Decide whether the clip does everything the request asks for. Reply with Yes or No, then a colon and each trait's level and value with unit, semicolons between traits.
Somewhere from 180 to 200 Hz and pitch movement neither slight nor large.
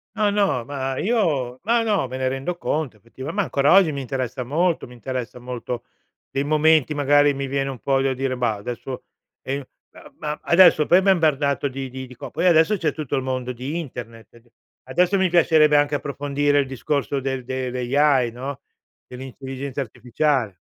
No: low, 135 Hz; average, 3.1 semitones